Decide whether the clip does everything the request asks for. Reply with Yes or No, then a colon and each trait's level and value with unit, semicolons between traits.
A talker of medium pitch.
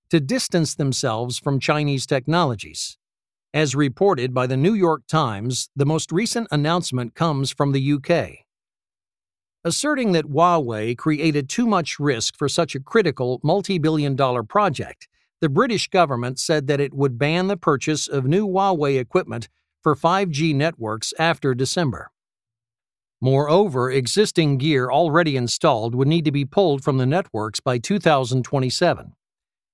Yes: medium, 145 Hz